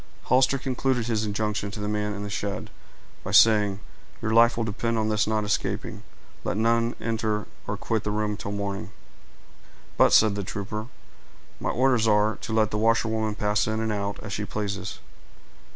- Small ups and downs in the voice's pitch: Yes, narrow, 1.5 semitones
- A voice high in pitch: No, low, 110 Hz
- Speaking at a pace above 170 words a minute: Yes, average, 180 wpm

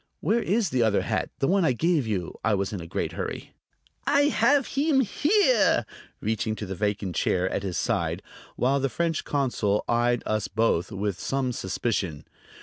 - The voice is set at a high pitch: No, low, 120 Hz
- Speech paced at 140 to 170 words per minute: No, average, 180 wpm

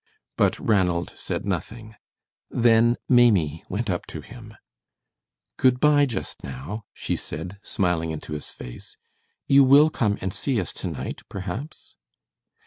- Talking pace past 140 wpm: No, slow, 135 wpm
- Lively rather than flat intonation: Yes, wide, 5.7 semitones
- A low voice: Yes, low, 105 Hz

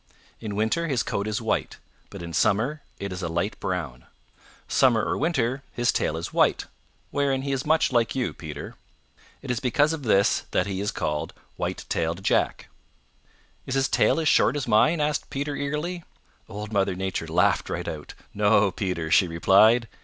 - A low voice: Yes, low, 110 Hz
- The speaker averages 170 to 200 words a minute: Yes, average, 180 wpm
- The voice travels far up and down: Yes, wide, 6.5 semitones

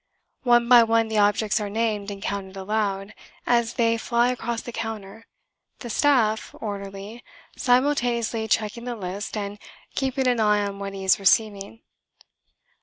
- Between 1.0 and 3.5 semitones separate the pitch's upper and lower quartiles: Yes, average, 2.8 semitones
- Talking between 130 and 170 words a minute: Yes, average, 150 wpm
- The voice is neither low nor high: No, high, 220 Hz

